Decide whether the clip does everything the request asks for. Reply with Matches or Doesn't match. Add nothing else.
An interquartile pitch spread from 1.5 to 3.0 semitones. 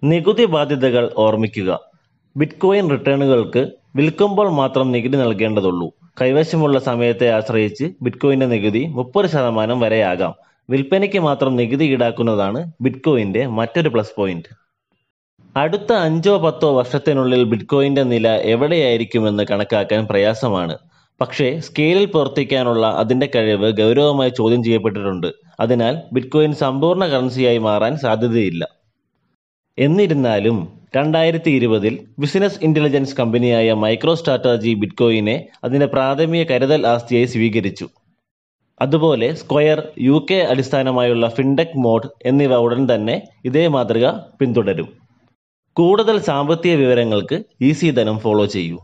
Doesn't match